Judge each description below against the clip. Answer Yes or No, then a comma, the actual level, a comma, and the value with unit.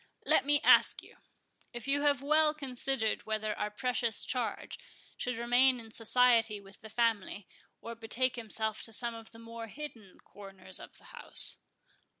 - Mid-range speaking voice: No, high, 230 Hz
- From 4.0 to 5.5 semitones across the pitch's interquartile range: No, narrow, 2.6 semitones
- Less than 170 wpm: Yes, average, 160 wpm